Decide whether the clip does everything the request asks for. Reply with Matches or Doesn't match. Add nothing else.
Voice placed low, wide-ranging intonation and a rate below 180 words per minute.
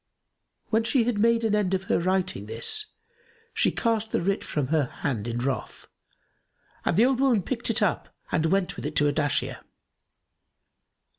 Doesn't match